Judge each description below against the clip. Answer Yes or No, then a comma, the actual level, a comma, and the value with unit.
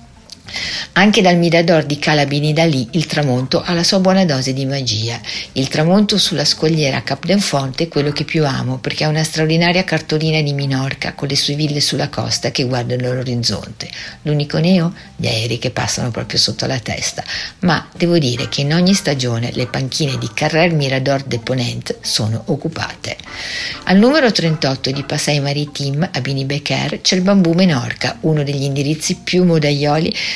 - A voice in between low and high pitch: Yes, medium, 145 Hz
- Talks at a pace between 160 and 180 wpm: Yes, fast, 170 wpm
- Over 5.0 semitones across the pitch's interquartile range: No, average, 4.0 semitones